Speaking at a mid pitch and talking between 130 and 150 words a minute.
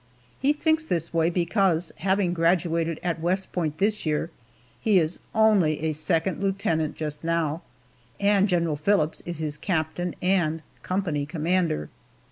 Yes: medium, 170 Hz; average, 140 wpm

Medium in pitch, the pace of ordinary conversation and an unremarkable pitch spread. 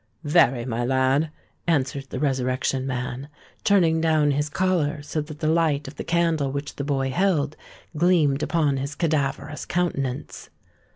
Yes: medium, 145 Hz; average, 150 wpm; average, 3.2 semitones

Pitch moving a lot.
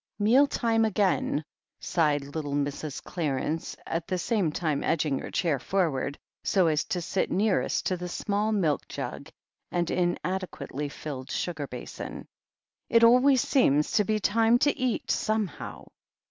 Yes: wide, 6.3 semitones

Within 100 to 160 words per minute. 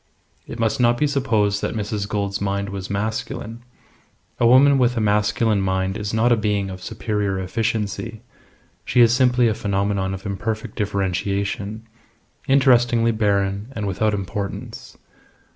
Yes: average, 145 wpm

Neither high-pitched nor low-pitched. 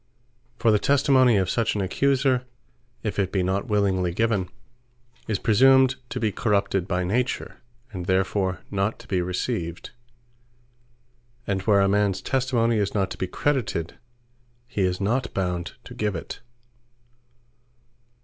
No: low, 100 Hz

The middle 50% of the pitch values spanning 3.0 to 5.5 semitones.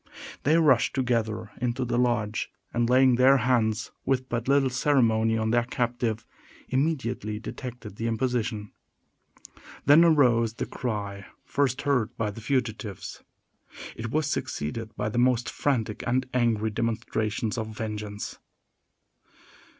No: narrow, 2.6 semitones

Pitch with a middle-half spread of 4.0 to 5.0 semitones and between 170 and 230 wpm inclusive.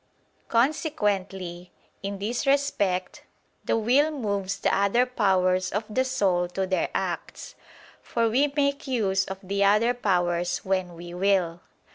No: average, 4.6 semitones; slow, 135 wpm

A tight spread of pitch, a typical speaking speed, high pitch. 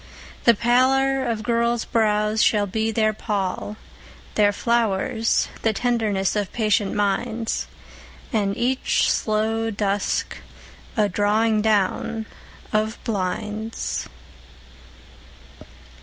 No: narrow, 1.9 semitones; slow, 95 wpm; high, 220 Hz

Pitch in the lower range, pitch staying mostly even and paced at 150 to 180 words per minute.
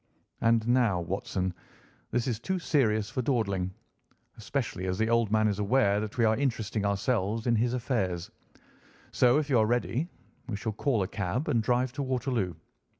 No: low, 115 Hz; average, 3.6 semitones; average, 175 wpm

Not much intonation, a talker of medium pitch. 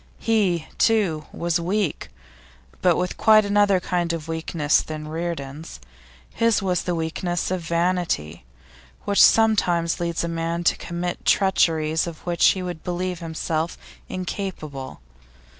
Yes: narrow, 2.3 semitones; medium, 170 Hz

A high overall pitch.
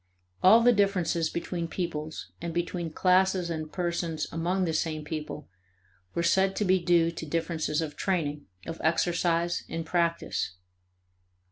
No: medium, 170 Hz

